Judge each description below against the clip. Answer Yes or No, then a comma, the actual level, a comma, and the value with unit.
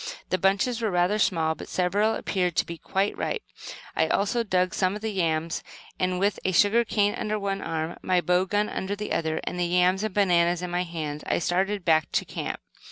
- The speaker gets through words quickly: Yes, fast, 215 wpm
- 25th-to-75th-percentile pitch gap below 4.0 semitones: Yes, average, 2.8 semitones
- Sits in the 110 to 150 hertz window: No, medium, 185 Hz